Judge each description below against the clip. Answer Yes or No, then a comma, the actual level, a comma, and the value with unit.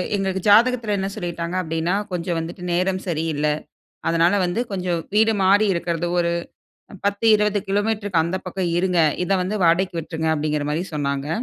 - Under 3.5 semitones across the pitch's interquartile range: Yes, average, 3.0 semitones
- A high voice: No, medium, 180 Hz